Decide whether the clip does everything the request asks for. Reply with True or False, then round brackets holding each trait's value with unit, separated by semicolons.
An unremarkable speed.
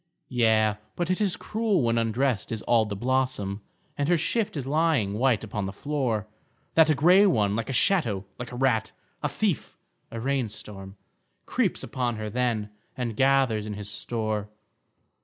True (175 wpm)